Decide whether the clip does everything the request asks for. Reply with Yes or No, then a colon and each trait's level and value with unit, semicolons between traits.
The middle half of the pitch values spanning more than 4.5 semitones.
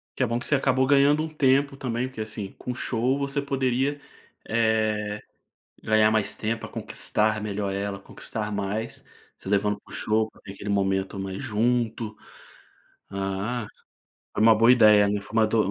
No: average, 3.5 semitones